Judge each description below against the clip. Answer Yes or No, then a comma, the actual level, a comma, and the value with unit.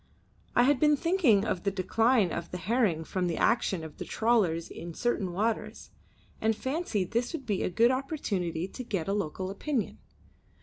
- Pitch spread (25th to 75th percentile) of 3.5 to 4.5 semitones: No, average, 5.3 semitones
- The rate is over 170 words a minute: Yes, average, 180 wpm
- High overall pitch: Yes, high, 210 Hz